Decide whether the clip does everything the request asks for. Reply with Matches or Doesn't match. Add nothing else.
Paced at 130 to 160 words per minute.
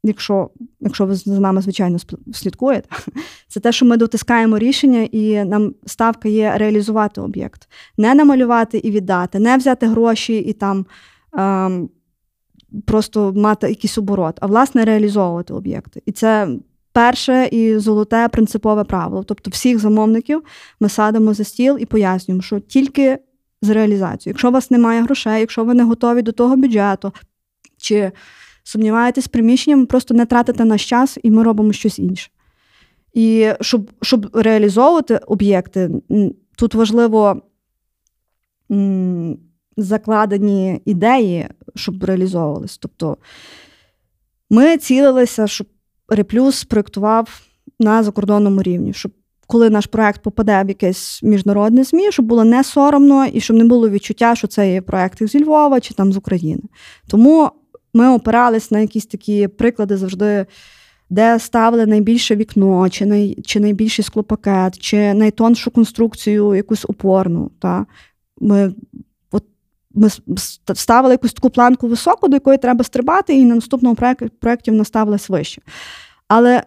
Matches